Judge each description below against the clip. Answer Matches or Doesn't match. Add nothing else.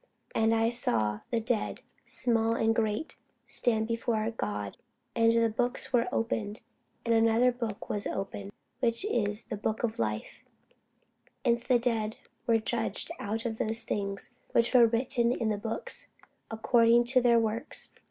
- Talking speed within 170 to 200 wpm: Doesn't match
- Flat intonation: Matches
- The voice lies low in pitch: Doesn't match